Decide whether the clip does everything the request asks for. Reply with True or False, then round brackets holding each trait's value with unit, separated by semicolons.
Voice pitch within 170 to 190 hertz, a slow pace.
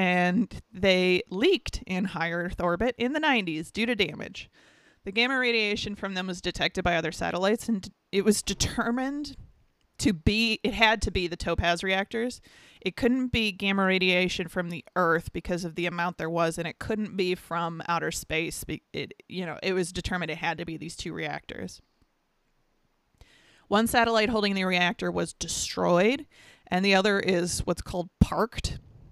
False (185 Hz; 170 wpm)